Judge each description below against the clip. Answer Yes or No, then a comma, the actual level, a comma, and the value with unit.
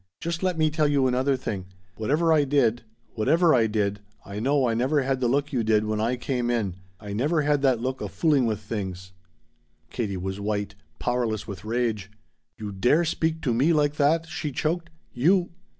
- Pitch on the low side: Yes, low, 125 Hz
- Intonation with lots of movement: Yes, wide, 5.7 semitones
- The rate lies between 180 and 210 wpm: Yes, average, 195 wpm